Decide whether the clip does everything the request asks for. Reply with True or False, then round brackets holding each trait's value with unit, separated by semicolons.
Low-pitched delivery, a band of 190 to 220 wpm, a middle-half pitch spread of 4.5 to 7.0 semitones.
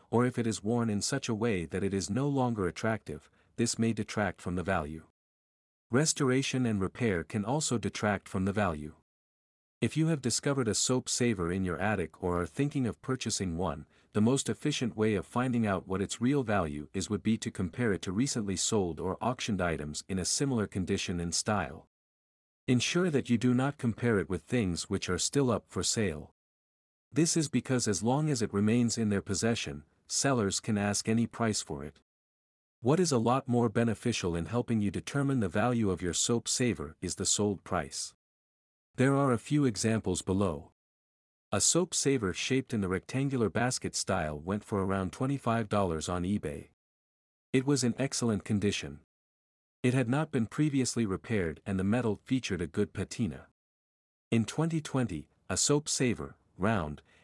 False (105 Hz; 180 wpm; 5.2 semitones)